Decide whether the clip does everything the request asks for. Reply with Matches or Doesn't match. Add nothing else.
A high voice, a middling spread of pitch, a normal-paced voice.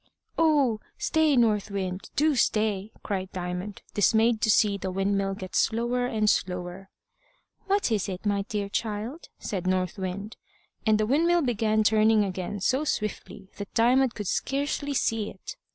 Matches